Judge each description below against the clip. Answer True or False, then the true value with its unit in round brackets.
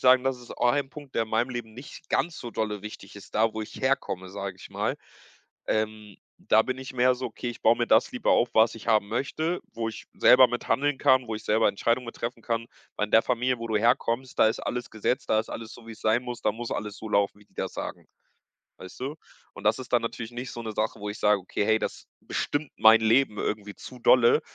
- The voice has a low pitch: True (115 Hz)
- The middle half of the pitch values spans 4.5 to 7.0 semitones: False (2.7 semitones)